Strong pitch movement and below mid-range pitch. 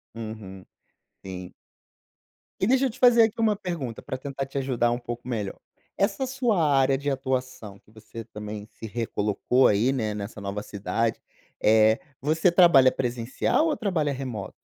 Yes: wide, 6.9 semitones; low, 130 Hz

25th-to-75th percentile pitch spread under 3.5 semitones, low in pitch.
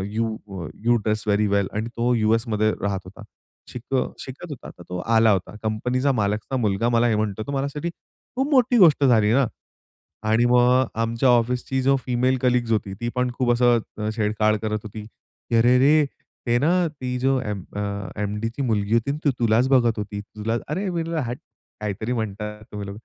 Yes: average, 3.0 semitones; low, 115 Hz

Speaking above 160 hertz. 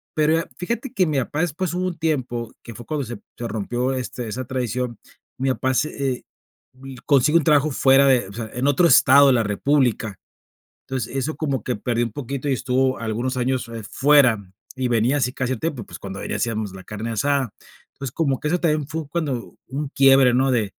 No: low, 130 Hz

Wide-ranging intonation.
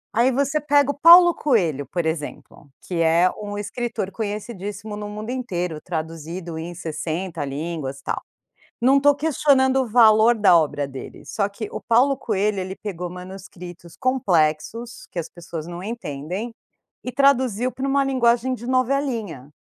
Yes: wide, 7.0 semitones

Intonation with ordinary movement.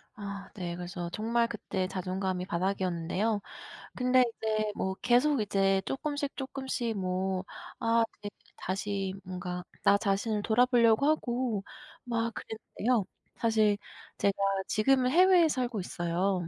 Yes: average, 4.2 semitones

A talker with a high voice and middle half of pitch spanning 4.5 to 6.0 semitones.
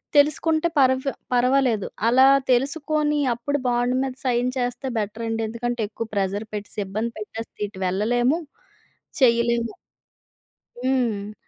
No: high, 240 Hz; average, 2.9 semitones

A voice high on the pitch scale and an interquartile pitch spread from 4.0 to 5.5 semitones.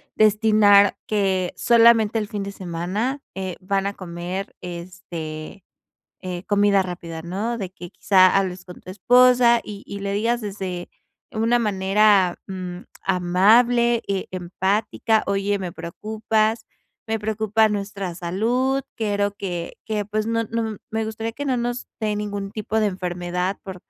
No: high, 200 Hz; average, 3.1 semitones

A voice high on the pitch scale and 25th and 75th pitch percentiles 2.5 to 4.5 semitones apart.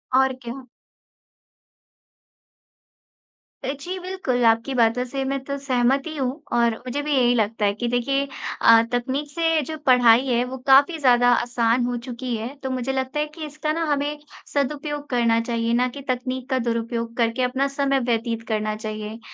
Yes: very high, 250 Hz; average, 2.9 semitones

